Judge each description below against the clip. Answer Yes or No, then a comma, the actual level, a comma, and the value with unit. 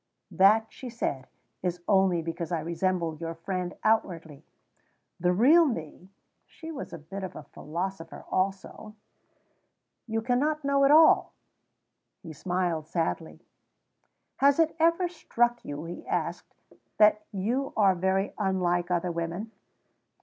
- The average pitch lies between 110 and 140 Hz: No, high, 190 Hz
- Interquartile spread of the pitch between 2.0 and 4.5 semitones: No, average, 5.3 semitones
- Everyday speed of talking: No, slow, 130 wpm